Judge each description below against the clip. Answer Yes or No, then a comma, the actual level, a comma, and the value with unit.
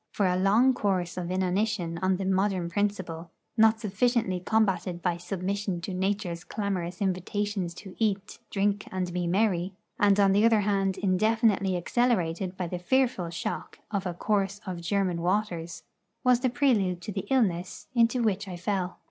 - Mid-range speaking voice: No, high, 195 Hz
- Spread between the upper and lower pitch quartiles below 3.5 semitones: Yes, average, 2.7 semitones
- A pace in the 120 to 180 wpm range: Yes, average, 165 wpm